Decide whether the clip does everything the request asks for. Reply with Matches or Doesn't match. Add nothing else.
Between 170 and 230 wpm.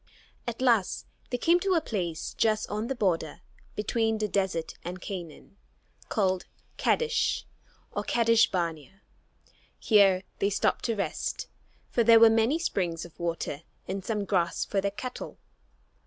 Doesn't match